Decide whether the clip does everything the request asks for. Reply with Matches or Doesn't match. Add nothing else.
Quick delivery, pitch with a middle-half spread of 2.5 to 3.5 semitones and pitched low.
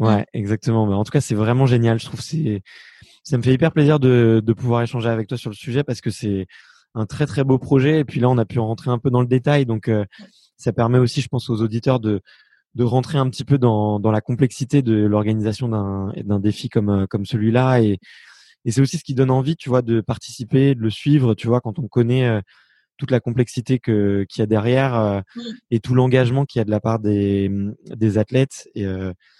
Matches